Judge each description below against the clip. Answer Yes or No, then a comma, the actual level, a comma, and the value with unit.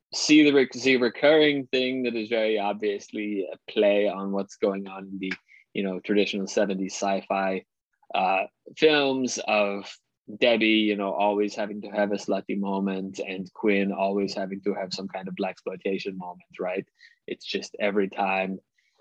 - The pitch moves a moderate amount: No, narrow, 2.0 semitones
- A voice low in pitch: Yes, low, 100 Hz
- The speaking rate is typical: Yes, average, 160 wpm